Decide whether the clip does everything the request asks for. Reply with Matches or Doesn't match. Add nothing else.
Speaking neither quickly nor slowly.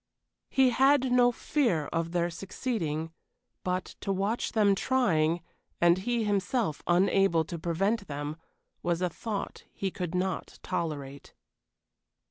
Doesn't match